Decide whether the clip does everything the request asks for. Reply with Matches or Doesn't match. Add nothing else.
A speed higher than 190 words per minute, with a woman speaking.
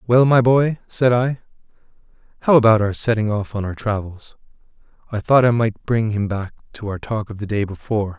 Doesn't match